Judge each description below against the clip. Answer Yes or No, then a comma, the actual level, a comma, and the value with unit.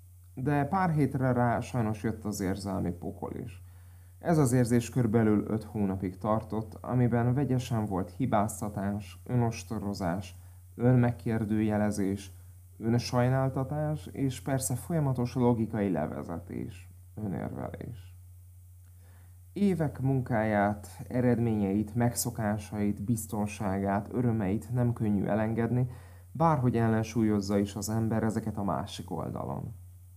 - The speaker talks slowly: Yes, slow, 95 wpm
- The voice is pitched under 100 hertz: No, low, 110 Hz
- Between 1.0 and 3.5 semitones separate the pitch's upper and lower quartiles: No, average, 4.0 semitones